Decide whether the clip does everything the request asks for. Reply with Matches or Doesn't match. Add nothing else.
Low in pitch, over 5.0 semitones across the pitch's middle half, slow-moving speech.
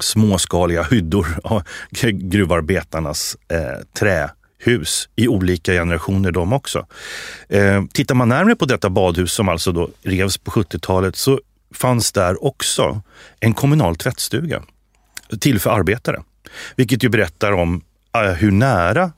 Doesn't match